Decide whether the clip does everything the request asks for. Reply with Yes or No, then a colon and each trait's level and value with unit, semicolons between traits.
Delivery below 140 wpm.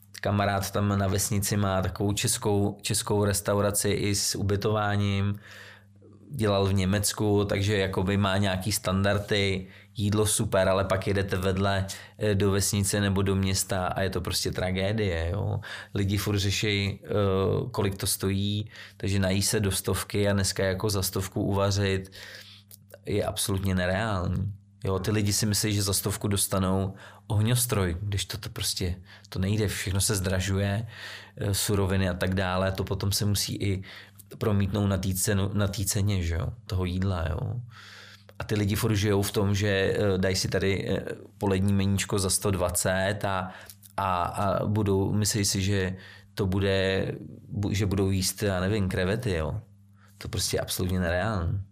No: average, 150 wpm